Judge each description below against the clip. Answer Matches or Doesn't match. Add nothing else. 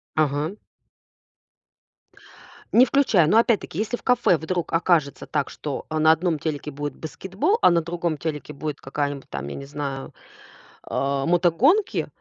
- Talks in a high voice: Doesn't match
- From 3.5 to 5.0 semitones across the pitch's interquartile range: Matches